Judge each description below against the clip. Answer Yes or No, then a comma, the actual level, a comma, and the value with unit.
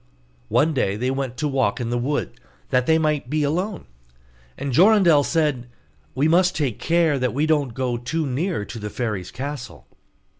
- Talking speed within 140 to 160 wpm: No, average, 180 wpm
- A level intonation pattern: No, average, 4.4 semitones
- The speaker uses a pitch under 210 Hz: Yes, medium, 140 Hz